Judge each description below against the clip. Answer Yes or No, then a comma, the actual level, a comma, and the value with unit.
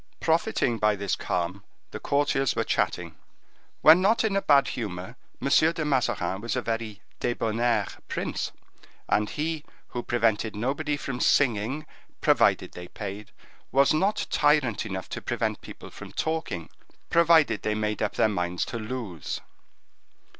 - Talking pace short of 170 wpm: Yes, average, 145 wpm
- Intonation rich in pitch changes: Yes, wide, 6.1 semitones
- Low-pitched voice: Yes, low, 120 Hz